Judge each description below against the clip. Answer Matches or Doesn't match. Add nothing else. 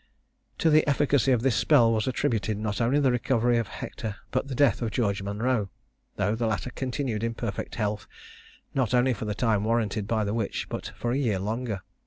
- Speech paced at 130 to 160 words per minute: Doesn't match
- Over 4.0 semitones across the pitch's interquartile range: Doesn't match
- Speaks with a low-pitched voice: Matches